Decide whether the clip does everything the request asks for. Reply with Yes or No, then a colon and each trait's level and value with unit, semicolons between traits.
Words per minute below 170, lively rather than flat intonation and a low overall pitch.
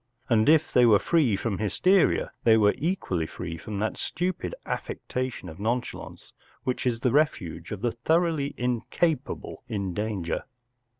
Yes: average, 145 wpm; wide, 6.2 semitones; low, 120 Hz